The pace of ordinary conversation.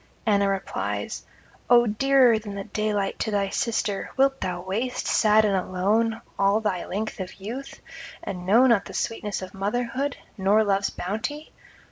Yes: average, 155 wpm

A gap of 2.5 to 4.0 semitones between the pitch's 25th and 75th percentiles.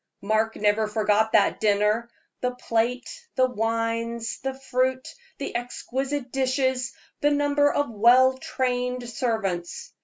Yes: average, 2.8 semitones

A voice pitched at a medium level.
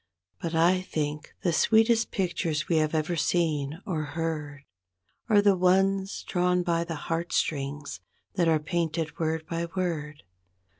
Yes: medium, 165 Hz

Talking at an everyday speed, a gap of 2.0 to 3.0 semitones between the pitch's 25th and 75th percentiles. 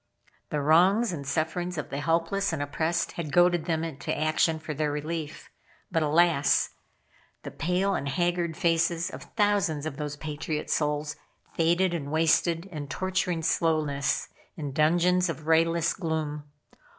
Yes: average, 145 wpm; narrow, 2.5 semitones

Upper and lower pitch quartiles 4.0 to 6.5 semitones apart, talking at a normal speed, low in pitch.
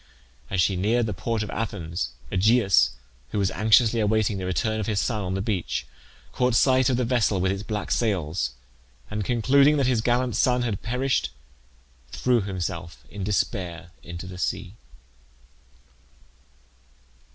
Yes: average, 4.4 semitones; average, 150 wpm; low, 105 Hz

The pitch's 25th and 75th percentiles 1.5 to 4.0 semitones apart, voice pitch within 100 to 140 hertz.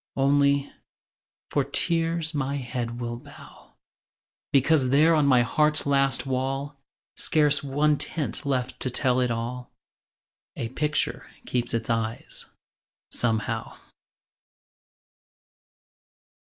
Yes: average, 3.0 semitones; low, 135 Hz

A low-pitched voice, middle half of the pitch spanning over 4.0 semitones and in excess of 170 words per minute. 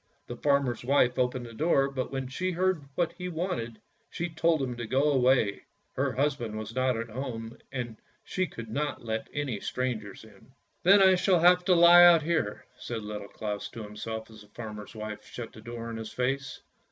Yes: low, 125 Hz; average, 5.2 semitones; average, 200 wpm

